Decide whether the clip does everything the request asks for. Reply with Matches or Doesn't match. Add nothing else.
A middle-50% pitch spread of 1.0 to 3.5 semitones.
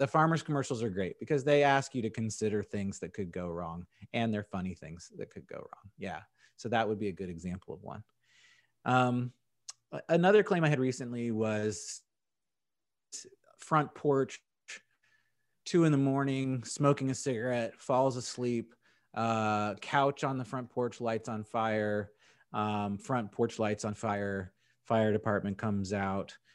Doesn't match